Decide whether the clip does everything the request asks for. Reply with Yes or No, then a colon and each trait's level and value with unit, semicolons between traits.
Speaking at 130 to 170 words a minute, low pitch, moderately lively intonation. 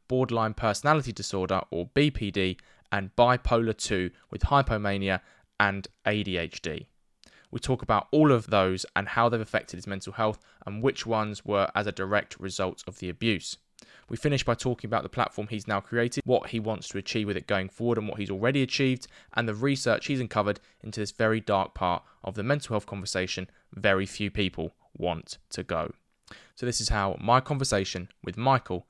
No: average, 185 wpm; low, 105 Hz; average, 3.5 semitones